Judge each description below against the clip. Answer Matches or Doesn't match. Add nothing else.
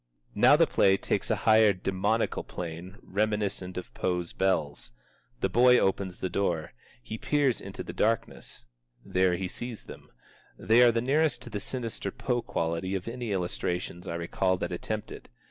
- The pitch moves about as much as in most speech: Matches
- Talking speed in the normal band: Matches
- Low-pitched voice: Matches